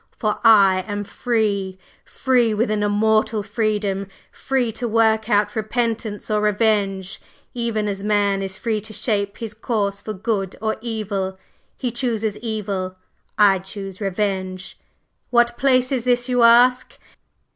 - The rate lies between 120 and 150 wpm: Yes, average, 140 wpm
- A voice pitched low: No, high, 215 Hz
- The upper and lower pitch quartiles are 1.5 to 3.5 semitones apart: Yes, narrow, 2.5 semitones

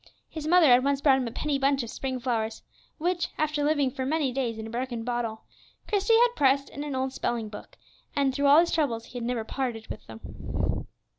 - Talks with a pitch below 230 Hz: No, very high, 265 Hz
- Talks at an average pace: No, fast, 220 wpm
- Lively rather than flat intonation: No, average, 3.7 semitones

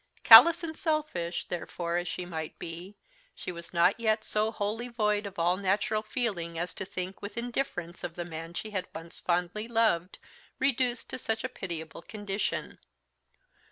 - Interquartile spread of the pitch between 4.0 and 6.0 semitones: Yes, average, 4.6 semitones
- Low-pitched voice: No, high, 195 Hz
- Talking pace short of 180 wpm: Yes, average, 165 wpm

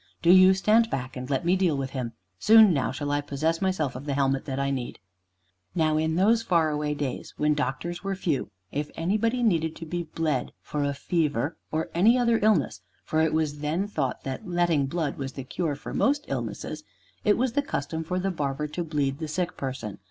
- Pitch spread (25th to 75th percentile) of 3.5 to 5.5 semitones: Yes, average, 4.5 semitones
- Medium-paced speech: No, fast, 210 wpm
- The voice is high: No, medium, 155 Hz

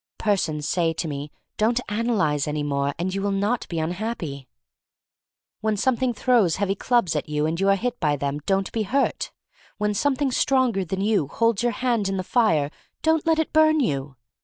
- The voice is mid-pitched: No, high, 195 Hz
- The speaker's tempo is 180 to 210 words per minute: Yes, average, 190 wpm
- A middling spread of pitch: No, wide, 7.1 semitones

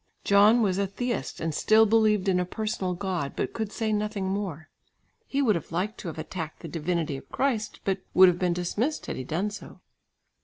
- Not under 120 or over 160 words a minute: No, fast, 205 wpm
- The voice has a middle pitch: No, high, 195 Hz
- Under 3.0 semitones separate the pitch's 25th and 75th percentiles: No, average, 3.8 semitones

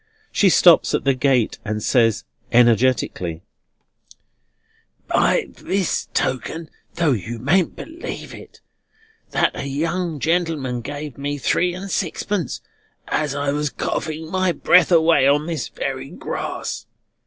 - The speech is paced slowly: Yes, slow, 125 wpm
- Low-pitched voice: No, medium, 150 Hz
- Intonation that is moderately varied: Yes, average, 4.8 semitones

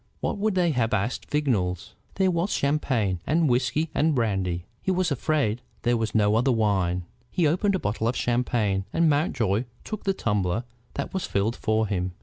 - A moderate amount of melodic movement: No, wide, 7.1 semitones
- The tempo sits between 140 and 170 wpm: No, average, 180 wpm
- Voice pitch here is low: Yes, low, 120 Hz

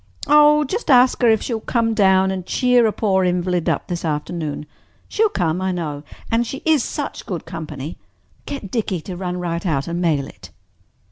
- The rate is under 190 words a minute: No, average, 195 wpm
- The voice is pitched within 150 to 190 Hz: Yes, medium, 185 Hz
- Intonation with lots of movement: Yes, wide, 6.0 semitones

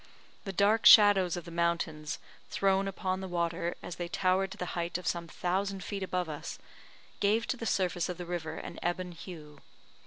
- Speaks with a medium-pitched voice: Yes, medium, 180 Hz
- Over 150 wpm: Yes, average, 190 wpm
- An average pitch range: No, narrow, 2.2 semitones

